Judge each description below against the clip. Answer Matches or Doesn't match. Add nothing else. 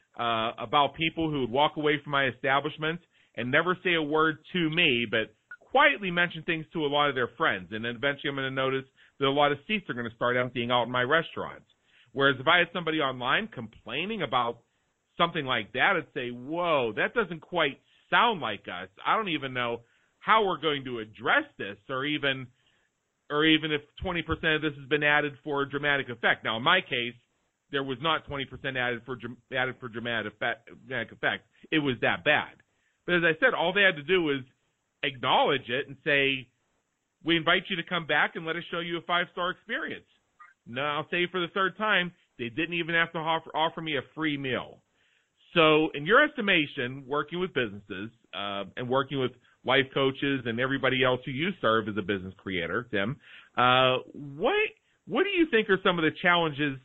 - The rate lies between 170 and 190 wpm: Doesn't match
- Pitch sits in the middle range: Matches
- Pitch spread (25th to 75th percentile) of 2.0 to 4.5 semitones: Doesn't match